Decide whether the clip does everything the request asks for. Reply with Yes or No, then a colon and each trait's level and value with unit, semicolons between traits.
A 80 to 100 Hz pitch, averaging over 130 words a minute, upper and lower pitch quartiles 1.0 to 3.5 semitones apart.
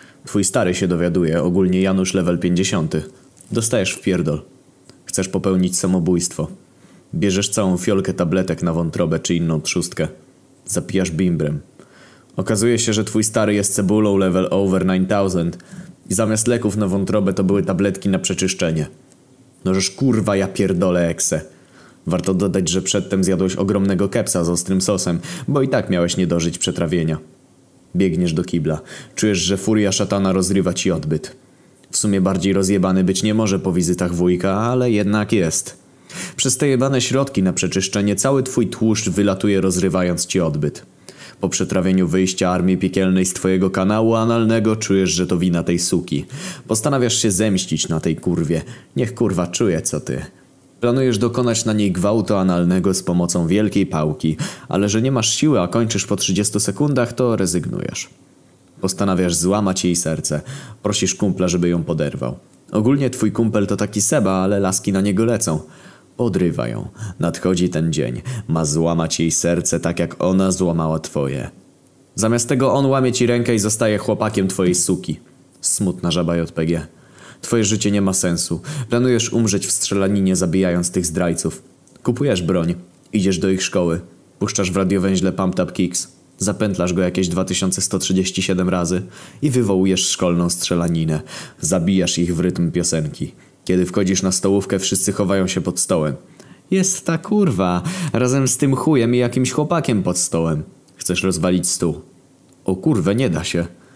Yes: very low, 95 Hz; average, 155 wpm; average, 3.2 semitones